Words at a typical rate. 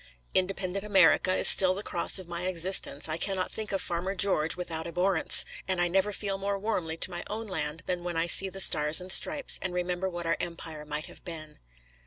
No: fast, 215 wpm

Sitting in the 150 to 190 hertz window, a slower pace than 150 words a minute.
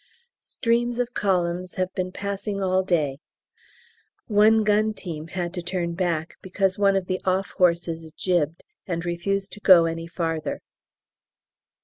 Yes: medium, 185 Hz; average, 140 wpm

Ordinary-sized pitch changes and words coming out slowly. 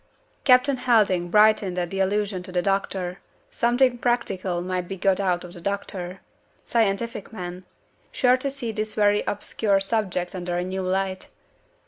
No: average, 3.2 semitones; average, 155 wpm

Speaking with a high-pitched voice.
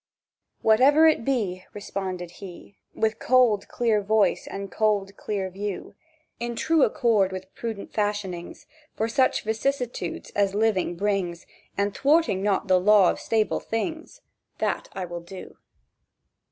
Yes: high, 205 Hz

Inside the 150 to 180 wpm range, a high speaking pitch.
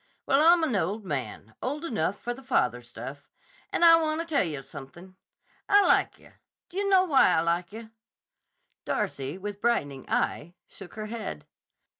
Yes: average, 170 wpm; high, 205 Hz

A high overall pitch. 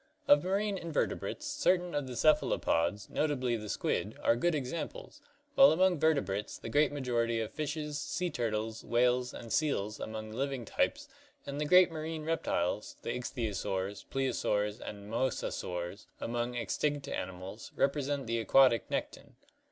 No: low, 125 Hz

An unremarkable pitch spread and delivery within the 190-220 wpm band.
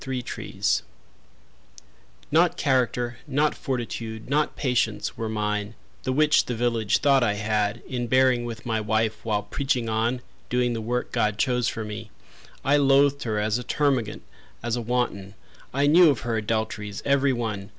No: average, 3.2 semitones; average, 160 wpm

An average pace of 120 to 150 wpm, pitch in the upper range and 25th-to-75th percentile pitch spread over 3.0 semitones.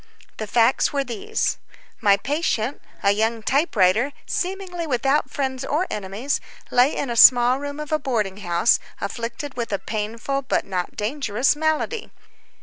Yes: average, 145 wpm; very high, 250 Hz; average, 5.1 semitones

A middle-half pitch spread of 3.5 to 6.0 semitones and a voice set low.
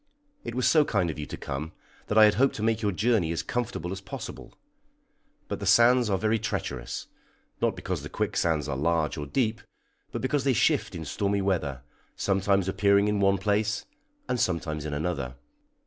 Yes: average, 5.3 semitones; low, 100 Hz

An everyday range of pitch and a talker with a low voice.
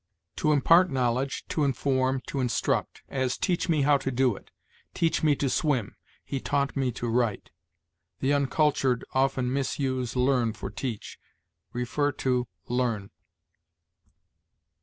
No: narrow, 2.2 semitones; low, 130 Hz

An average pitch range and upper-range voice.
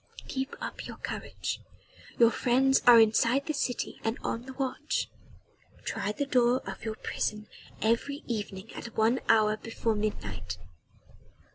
Yes: average, 3.4 semitones; high, 230 Hz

